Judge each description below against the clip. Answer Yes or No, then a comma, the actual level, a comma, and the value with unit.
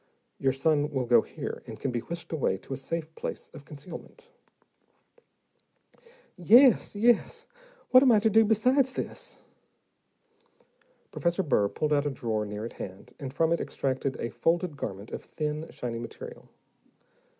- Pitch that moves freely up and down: Yes, wide, 6.6 semitones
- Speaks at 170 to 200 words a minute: No, average, 155 wpm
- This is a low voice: No, medium, 150 Hz